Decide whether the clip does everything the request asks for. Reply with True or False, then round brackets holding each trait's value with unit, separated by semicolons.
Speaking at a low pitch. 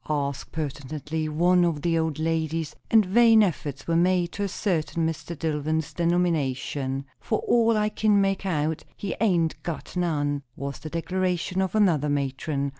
False (165 Hz)